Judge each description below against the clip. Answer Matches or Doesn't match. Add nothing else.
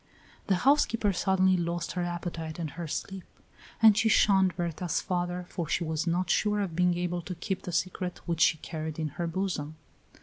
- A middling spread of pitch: Doesn't match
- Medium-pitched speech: Matches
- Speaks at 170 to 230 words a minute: Matches